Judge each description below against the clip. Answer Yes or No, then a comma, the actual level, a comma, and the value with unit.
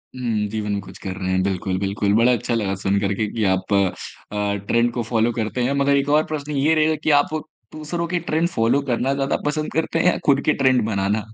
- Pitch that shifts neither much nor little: No, wide, 5.9 semitones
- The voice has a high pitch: No, low, 120 Hz